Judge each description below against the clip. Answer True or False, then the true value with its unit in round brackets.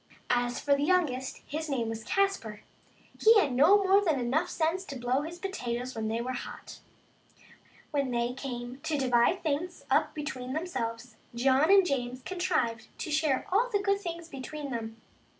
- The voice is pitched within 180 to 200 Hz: False (280 Hz)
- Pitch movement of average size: False (6.1 semitones)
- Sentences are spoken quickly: False (180 wpm)